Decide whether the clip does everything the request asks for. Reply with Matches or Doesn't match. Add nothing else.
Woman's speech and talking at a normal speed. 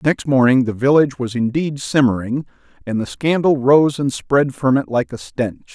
Doesn't match